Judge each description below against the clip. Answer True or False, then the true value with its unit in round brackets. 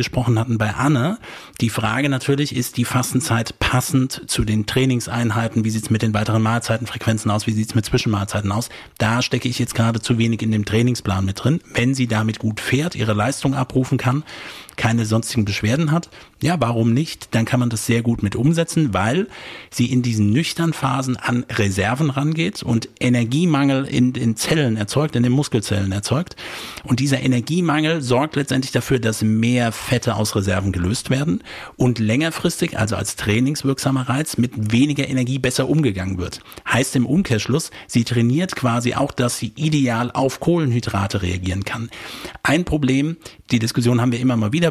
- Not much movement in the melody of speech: False (3.4 semitones)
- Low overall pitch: True (120 Hz)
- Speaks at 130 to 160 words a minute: False (175 wpm)